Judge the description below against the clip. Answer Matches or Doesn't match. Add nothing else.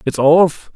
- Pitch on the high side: Doesn't match